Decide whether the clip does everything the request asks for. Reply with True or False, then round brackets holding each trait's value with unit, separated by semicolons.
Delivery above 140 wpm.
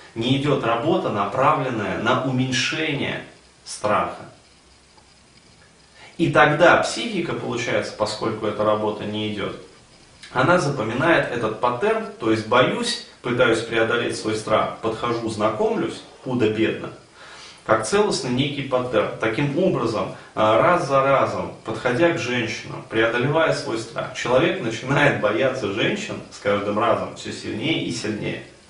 False (115 wpm)